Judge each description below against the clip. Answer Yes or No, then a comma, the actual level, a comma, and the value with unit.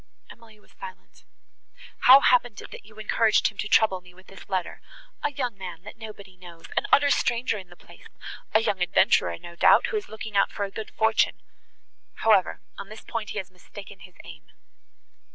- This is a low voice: No, high, 210 Hz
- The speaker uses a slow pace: No, average, 185 wpm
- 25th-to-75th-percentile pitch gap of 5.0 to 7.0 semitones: No, average, 3.3 semitones